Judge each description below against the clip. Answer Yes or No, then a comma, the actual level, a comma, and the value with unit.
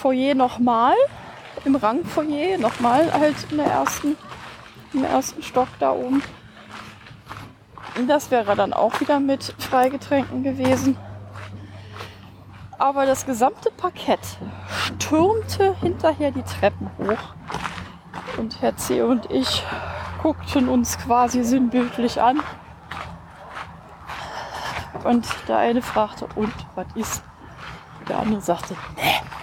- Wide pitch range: Yes, wide, 8.2 semitones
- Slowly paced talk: Yes, slow, 105 wpm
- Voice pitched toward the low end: No, very high, 250 Hz